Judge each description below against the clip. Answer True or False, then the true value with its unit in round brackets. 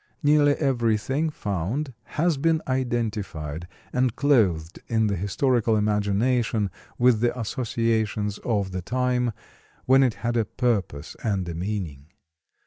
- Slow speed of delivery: True (125 wpm)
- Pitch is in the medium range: False (115 Hz)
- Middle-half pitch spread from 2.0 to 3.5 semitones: False (4.1 semitones)